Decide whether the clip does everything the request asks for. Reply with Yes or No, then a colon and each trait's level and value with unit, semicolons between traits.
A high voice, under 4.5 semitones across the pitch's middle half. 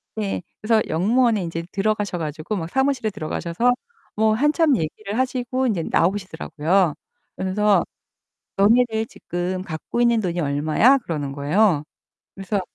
No: high, 200 Hz; average, 5.3 semitones